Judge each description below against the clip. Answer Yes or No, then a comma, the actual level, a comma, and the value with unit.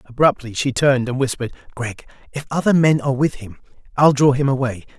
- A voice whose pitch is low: Yes, low, 130 Hz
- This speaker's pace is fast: No, average, 195 wpm